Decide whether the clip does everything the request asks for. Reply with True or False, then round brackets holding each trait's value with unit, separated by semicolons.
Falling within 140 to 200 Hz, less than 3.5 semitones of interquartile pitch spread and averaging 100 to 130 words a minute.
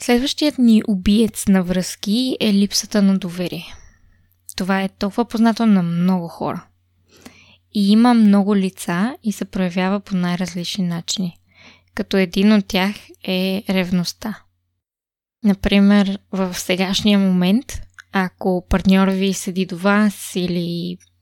True (190 Hz; 2.8 semitones; 120 wpm)